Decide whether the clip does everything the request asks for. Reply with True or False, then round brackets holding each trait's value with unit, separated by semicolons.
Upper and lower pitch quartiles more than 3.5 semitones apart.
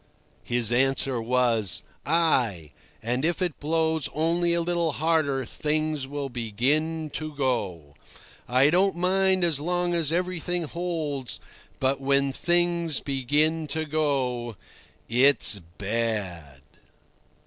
True (5.0 semitones)